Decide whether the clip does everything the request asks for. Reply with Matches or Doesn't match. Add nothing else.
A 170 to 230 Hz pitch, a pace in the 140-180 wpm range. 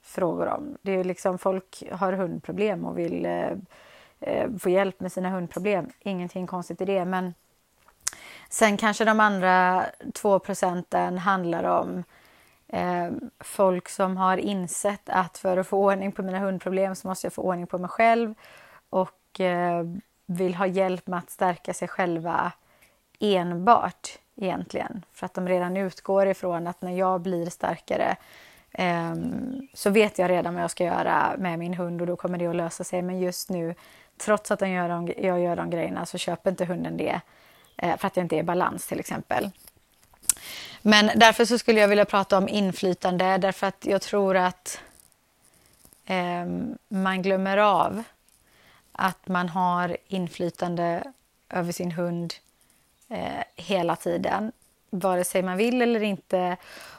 Matches